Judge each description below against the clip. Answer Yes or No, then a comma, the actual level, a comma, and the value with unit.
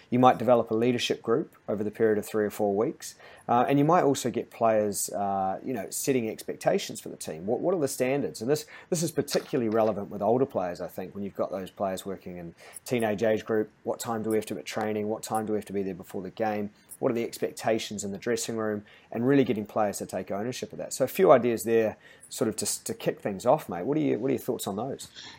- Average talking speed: No, fast, 265 wpm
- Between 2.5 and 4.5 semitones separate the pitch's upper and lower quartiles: Yes, average, 2.8 semitones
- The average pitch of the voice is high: No, low, 110 Hz